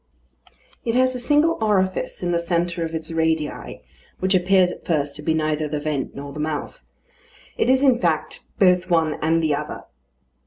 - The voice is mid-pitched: Yes, medium, 165 Hz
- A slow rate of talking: No, average, 185 wpm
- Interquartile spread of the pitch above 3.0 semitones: Yes, average, 3.5 semitones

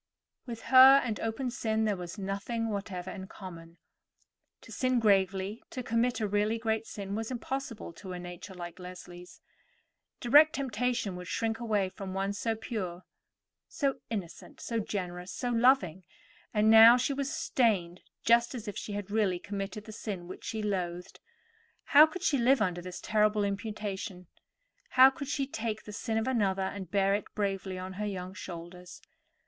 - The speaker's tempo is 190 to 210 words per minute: No, average, 170 wpm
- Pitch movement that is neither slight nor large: Yes, average, 3.8 semitones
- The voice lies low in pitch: No, high, 210 Hz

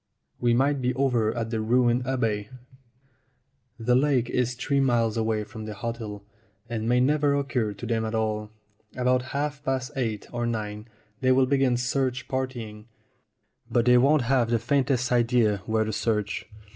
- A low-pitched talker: Yes, low, 120 Hz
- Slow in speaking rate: No, average, 165 wpm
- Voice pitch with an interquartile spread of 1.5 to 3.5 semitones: Yes, average, 2.7 semitones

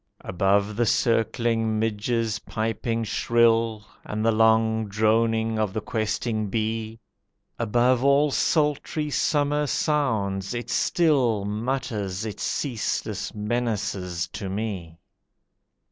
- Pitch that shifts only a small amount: Yes, narrow, 2.2 semitones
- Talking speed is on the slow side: Yes, slow, 100 wpm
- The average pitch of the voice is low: Yes, low, 110 Hz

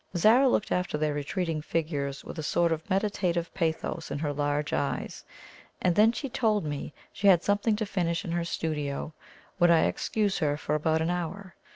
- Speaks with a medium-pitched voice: Yes, medium, 170 Hz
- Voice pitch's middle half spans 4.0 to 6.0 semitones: Yes, average, 4.4 semitones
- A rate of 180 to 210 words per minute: Yes, average, 190 wpm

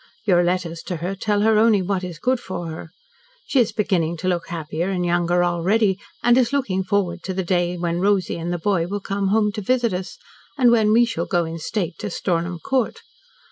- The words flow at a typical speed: No, fast, 220 wpm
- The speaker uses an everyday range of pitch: Yes, average, 3.4 semitones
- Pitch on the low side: No, medium, 185 Hz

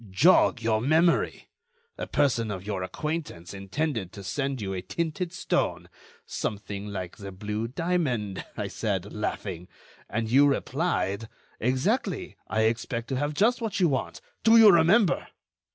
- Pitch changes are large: Yes, wide, 8.1 semitones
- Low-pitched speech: Yes, low, 120 Hz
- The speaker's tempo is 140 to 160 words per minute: Yes, average, 145 wpm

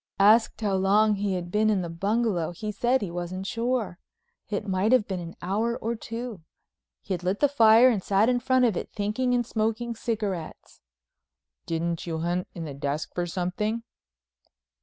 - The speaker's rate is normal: Yes, average, 180 wpm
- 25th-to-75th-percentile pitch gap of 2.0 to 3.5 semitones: No, average, 4.3 semitones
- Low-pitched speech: No, high, 205 Hz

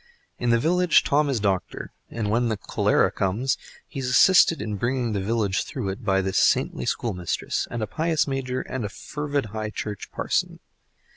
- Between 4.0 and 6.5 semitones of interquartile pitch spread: Yes, average, 4.7 semitones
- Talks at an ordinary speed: Yes, average, 185 wpm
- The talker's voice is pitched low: Yes, low, 115 Hz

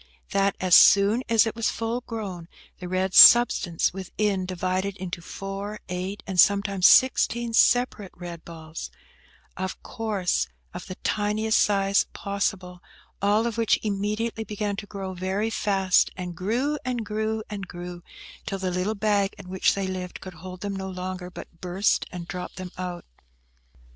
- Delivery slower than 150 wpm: No, average, 155 wpm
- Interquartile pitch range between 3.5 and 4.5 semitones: No, average, 2.7 semitones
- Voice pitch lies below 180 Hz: No, high, 195 Hz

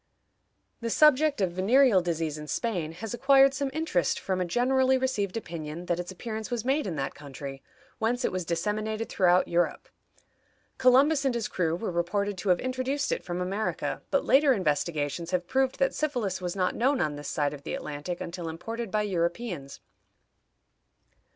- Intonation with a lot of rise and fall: Yes, wide, 6.8 semitones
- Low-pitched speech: No, high, 195 Hz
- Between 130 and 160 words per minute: No, average, 175 wpm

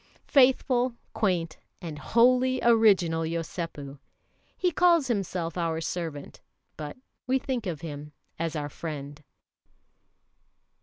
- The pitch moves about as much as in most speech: No, wide, 7.6 semitones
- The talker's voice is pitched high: No, medium, 170 Hz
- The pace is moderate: No, slow, 105 wpm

